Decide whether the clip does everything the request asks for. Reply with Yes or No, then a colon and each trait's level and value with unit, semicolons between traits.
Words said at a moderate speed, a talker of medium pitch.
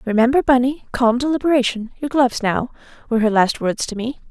No: average, 155 wpm; high, 245 Hz